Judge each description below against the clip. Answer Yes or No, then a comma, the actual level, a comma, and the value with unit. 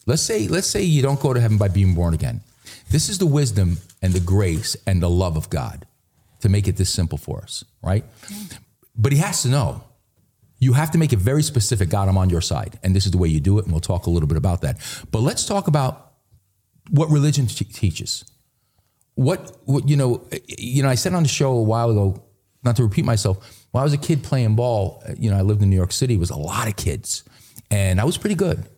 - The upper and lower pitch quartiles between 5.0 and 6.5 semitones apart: Yes, wide, 5.6 semitones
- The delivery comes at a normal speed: No, fast, 245 wpm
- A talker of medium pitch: No, low, 115 Hz